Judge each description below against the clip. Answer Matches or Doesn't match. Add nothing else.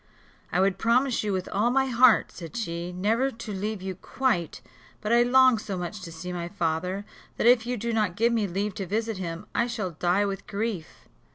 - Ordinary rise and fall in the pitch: Matches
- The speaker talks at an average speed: Doesn't match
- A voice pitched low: Doesn't match